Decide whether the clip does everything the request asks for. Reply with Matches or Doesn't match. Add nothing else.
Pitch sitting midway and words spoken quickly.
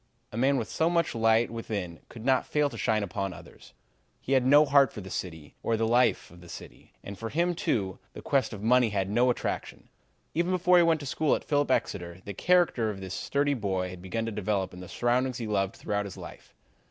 Doesn't match